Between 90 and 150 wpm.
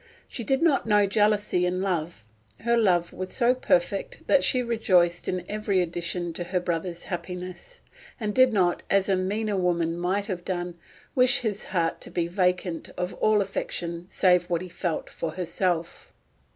No: average, 170 wpm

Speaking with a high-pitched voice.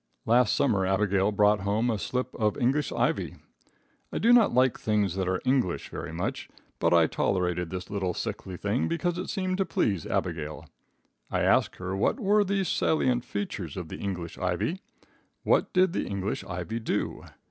No: low, 105 Hz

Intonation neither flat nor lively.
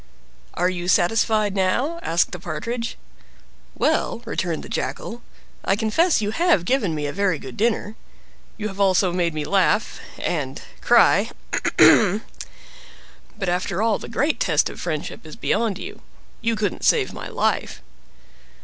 Yes: average, 4.2 semitones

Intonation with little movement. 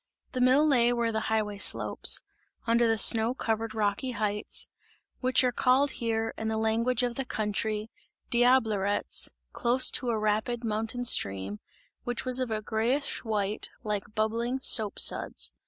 Yes: narrow, 2.3 semitones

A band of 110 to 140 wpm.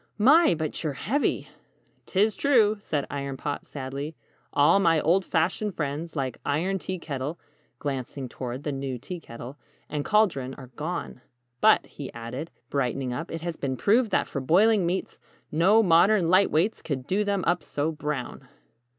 No: average, 165 wpm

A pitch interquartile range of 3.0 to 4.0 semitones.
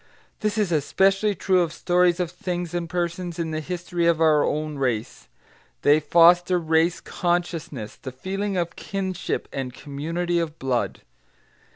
No: narrow, 2.5 semitones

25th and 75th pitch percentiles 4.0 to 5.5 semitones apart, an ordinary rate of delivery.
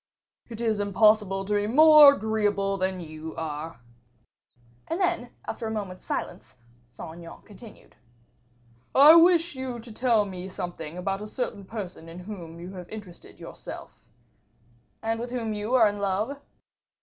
Yes: average, 4.3 semitones; average, 150 wpm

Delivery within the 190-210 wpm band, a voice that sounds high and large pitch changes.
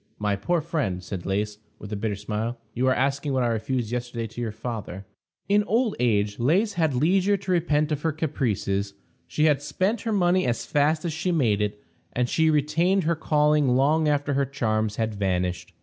No: average, 195 wpm; low, 135 Hz; wide, 6.7 semitones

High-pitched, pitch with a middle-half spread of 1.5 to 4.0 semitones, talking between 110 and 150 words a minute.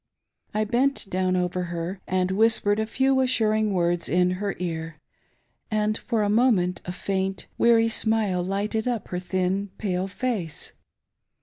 Yes: high, 195 Hz; average, 3.4 semitones; average, 145 wpm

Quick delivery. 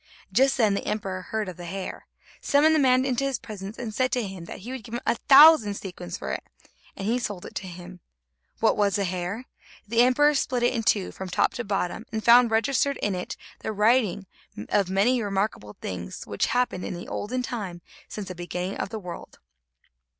Yes: fast, 210 wpm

